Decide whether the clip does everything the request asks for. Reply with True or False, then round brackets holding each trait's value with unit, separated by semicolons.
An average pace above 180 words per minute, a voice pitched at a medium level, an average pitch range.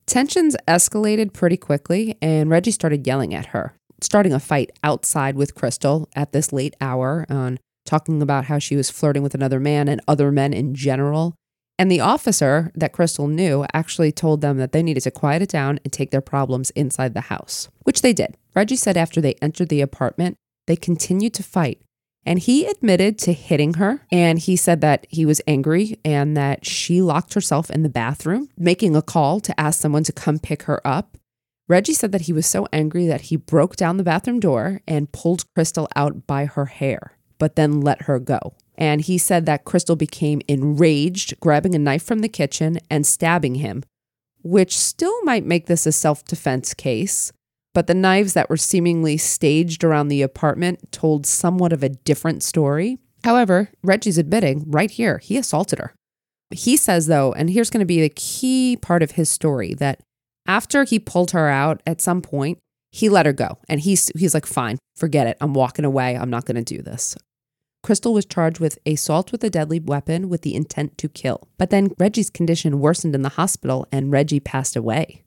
True (195 wpm; 155 Hz; 4.0 semitones)